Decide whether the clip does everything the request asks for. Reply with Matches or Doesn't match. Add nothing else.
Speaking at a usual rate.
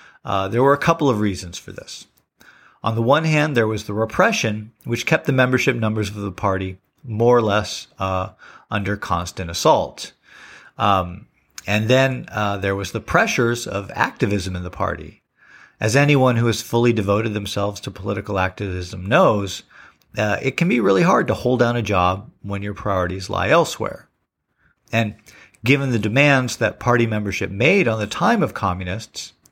Matches